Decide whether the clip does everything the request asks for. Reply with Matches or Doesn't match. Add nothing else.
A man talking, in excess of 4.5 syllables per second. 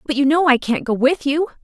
Doesn't match